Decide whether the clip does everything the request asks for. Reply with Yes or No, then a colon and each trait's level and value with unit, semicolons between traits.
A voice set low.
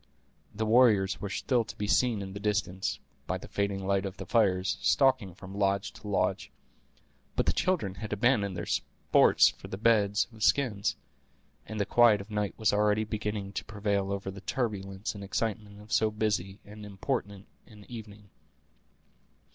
Yes: low, 105 Hz